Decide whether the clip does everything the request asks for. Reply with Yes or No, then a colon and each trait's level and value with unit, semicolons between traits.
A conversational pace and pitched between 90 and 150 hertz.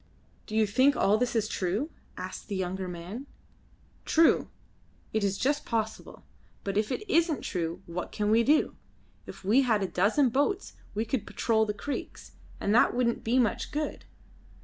No: average, 170 wpm; high, 220 Hz